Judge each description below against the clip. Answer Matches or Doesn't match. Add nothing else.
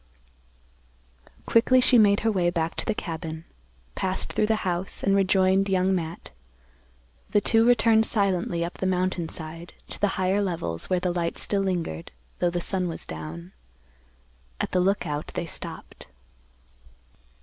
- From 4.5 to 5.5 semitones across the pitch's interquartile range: Doesn't match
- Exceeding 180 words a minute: Doesn't match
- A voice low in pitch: Doesn't match